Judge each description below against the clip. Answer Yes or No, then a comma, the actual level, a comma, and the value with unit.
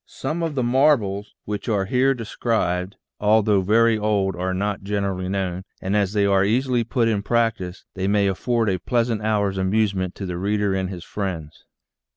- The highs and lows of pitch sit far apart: No, average, 3.1 semitones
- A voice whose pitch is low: Yes, low, 100 Hz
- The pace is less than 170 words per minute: No, average, 180 wpm